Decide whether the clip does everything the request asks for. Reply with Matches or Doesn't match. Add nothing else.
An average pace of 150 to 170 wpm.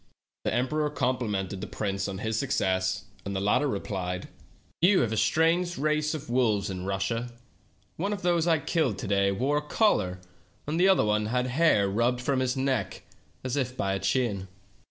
Doesn't match